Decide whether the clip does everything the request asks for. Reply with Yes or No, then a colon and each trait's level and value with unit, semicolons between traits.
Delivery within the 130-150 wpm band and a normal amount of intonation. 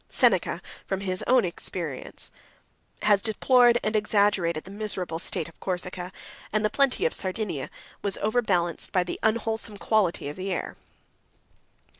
Yes: average, 145 wpm; average, 3.4 semitones